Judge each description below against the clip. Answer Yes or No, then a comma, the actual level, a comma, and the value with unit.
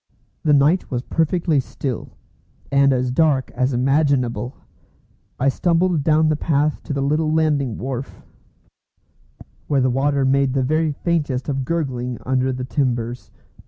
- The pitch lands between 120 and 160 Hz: Yes, medium, 140 Hz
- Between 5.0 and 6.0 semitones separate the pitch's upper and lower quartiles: No, average, 3.1 semitones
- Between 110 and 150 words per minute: Yes, average, 140 wpm